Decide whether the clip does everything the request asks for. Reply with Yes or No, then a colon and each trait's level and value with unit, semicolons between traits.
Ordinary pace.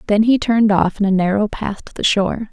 No: fast, 260 wpm